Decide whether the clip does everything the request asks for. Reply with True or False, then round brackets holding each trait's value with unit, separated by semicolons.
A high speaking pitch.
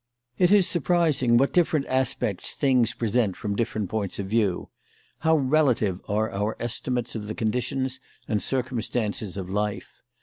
False (120 Hz)